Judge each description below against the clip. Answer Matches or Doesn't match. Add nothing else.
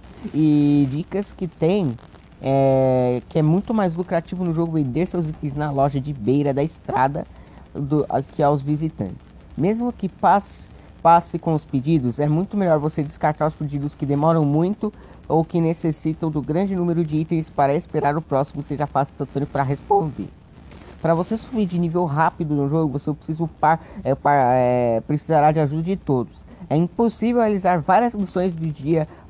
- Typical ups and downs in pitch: Matches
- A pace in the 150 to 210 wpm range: Matches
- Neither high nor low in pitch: Matches